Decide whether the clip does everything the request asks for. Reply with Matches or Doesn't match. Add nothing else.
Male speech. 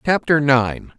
Matches